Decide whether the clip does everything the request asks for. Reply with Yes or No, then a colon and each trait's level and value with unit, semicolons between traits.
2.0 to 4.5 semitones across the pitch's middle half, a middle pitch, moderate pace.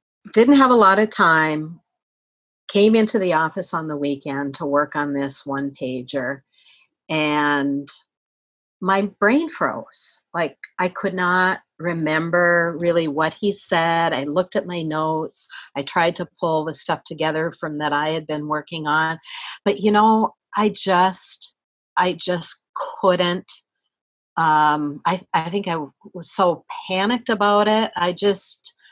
Yes: average, 4.2 semitones; medium, 165 Hz; average, 145 wpm